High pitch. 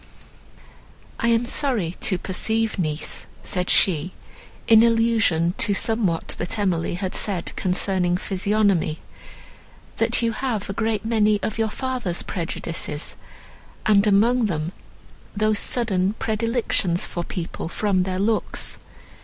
Yes: high, 200 Hz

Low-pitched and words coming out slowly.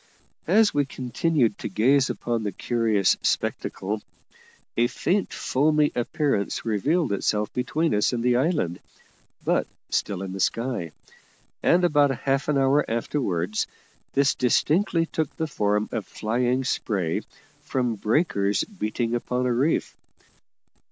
Yes: low, 125 Hz; slow, 130 wpm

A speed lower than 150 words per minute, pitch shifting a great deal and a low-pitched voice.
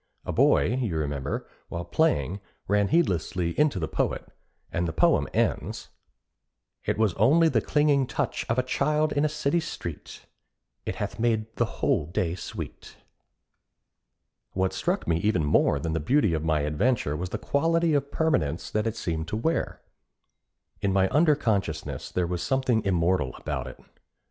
No: average, 165 wpm; wide, 9.0 semitones; low, 100 Hz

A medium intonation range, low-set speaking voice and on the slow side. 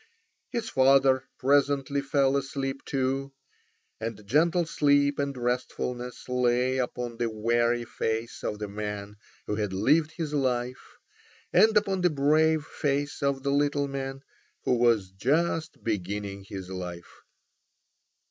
Yes: average, 3.8 semitones; low, 130 Hz; slow, 130 wpm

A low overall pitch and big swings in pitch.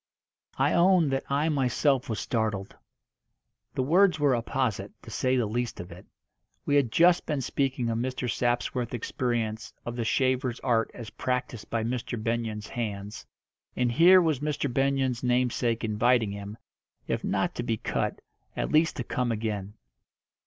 No: low, 125 Hz; average, 3.1 semitones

